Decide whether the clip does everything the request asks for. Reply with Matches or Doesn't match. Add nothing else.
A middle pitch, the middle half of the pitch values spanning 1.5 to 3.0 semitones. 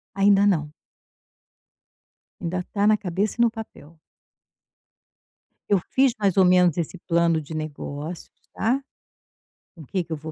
Doesn't match